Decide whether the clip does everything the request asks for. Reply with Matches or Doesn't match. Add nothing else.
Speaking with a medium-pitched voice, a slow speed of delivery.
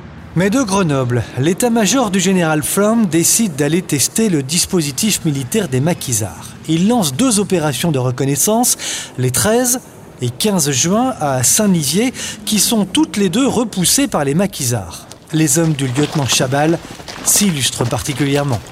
Matches